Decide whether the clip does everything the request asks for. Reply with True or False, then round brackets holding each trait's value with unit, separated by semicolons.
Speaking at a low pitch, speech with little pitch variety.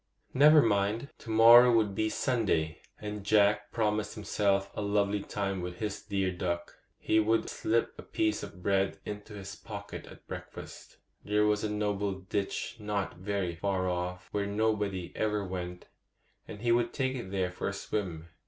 True (100 Hz; 2.0 semitones)